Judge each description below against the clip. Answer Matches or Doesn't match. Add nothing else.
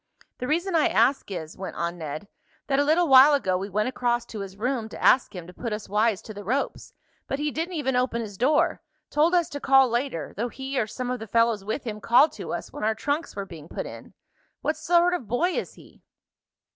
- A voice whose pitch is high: Matches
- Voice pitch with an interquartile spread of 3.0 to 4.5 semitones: Doesn't match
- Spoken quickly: Matches